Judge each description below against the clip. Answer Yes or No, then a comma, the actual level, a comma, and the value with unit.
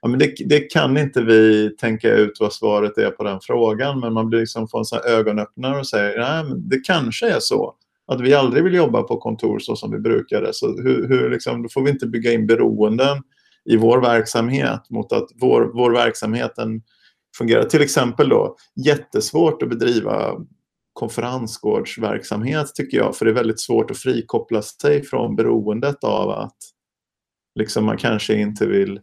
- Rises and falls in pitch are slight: No, average, 4.2 semitones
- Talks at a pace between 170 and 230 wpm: Yes, average, 175 wpm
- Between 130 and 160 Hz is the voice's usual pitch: No, low, 115 Hz